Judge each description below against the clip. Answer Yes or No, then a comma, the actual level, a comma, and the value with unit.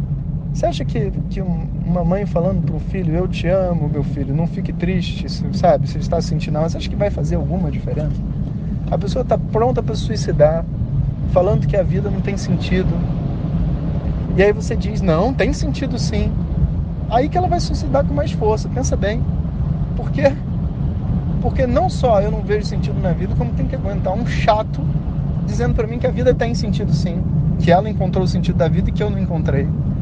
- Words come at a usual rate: No, fast, 200 wpm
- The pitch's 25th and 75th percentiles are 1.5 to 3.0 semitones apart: Yes, narrow, 2.6 semitones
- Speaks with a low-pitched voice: No, medium, 160 Hz